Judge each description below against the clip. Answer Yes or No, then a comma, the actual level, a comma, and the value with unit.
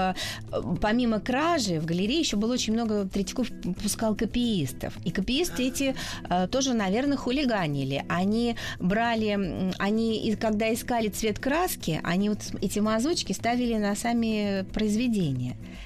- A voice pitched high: Yes, high, 215 Hz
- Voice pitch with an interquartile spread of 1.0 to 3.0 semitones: No, average, 3.8 semitones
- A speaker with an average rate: Yes, average, 120 wpm